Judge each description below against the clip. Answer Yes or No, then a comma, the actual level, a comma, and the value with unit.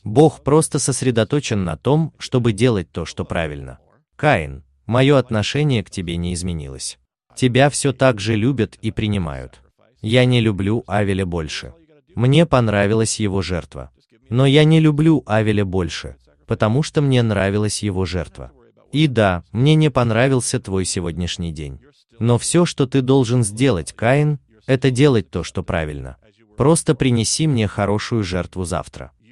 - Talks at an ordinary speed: Yes, average, 145 wpm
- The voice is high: No, low, 110 Hz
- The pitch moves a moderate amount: No, wide, 6.7 semitones